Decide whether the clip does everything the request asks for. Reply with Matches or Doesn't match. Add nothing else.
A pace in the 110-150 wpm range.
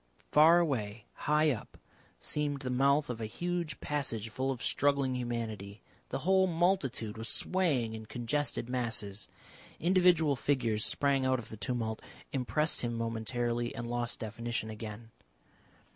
Matches